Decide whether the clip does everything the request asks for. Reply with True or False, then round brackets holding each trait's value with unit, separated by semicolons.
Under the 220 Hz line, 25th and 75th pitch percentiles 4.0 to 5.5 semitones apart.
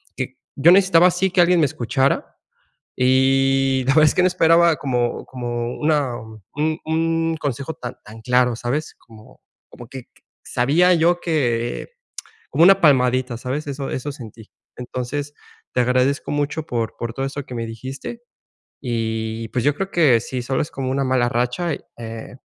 True (135 Hz; 4.5 semitones)